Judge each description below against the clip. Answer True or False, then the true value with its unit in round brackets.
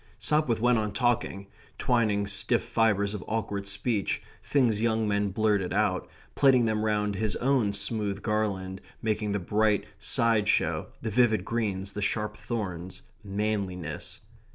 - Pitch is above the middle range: False (105 Hz)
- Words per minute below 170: True (140 wpm)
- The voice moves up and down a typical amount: False (2.1 semitones)